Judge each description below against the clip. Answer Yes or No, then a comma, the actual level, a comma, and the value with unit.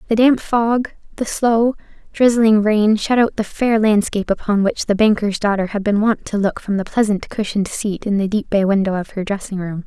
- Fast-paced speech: Yes, fast, 220 wpm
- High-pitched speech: Yes, high, 210 Hz